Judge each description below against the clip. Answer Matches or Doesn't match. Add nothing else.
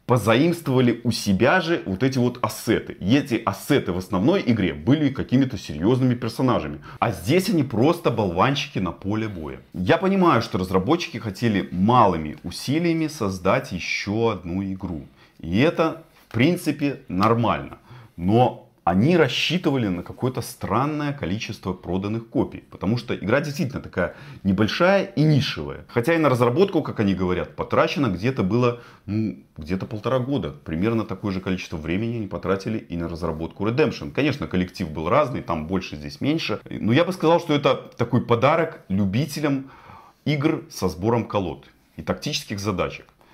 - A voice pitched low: Matches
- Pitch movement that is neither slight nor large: Doesn't match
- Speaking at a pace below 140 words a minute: Doesn't match